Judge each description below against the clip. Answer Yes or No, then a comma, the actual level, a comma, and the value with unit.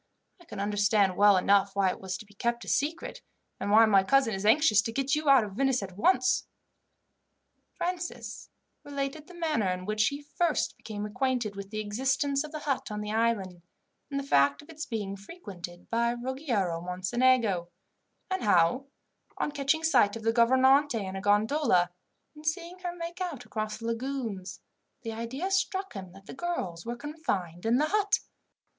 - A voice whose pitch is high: Yes, high, 230 Hz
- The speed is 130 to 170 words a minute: No, average, 180 wpm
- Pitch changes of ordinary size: No, wide, 6.2 semitones